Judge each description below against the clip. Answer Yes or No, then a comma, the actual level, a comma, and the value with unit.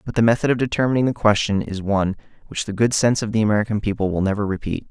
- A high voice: No, low, 110 Hz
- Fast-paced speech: Yes, fast, 245 wpm